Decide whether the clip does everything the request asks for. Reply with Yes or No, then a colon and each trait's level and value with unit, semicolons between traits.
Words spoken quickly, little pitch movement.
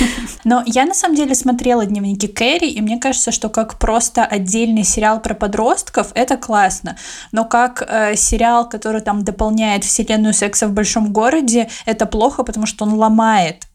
Yes: fast, 165 wpm; narrow, 1.7 semitones